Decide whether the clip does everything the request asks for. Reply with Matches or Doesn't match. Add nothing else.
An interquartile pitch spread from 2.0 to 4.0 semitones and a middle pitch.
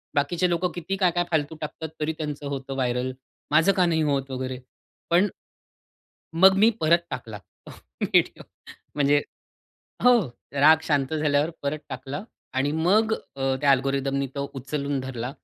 Matches